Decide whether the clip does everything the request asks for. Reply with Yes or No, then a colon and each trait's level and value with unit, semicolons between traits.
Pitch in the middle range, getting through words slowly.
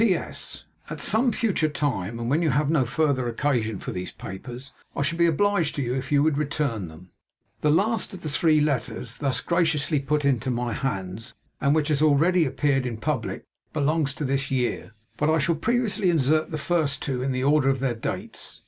No: medium, 145 Hz; average, 200 wpm